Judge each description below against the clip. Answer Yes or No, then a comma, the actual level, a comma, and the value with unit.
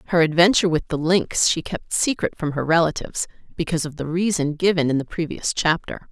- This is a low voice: No, medium, 165 Hz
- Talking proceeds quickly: No, average, 195 wpm